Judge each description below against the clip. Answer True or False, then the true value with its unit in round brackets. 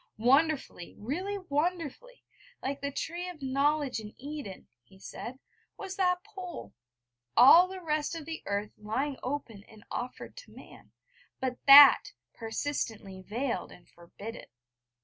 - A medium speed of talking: False (130 wpm)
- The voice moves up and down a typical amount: False (6.9 semitones)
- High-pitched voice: True (280 Hz)